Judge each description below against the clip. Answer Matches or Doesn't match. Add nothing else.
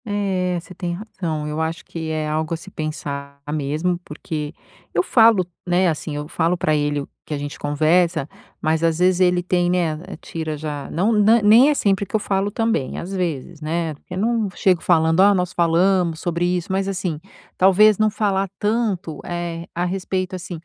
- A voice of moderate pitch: Matches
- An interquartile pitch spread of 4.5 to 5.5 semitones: Doesn't match